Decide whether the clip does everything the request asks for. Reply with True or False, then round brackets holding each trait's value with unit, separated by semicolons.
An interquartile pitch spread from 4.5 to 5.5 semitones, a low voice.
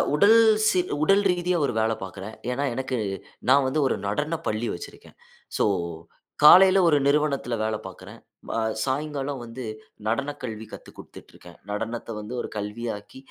True (5.2 semitones; 130 Hz)